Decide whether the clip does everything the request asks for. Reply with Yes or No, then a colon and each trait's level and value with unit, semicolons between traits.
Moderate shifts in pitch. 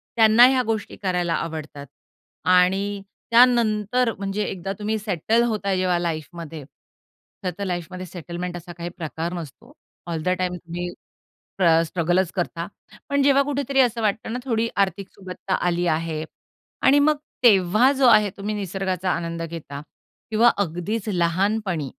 Yes: average, 4.2 semitones